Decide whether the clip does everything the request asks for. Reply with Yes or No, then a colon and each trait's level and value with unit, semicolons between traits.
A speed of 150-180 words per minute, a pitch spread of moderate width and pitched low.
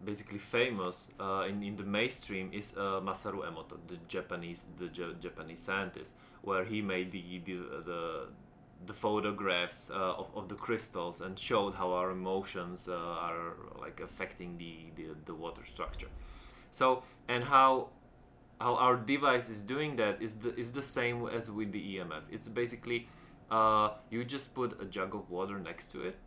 Yes: average, 170 wpm; average, 4.5 semitones; low, 105 Hz